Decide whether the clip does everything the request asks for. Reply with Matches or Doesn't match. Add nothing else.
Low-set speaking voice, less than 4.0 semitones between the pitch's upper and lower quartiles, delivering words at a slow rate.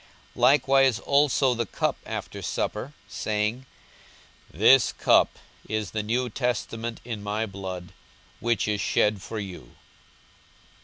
Matches